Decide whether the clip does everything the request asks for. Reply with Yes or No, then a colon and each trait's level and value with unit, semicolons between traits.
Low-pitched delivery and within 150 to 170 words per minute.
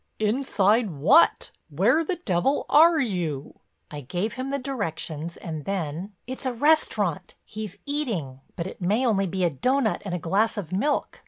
No: high, 205 Hz; average, 165 wpm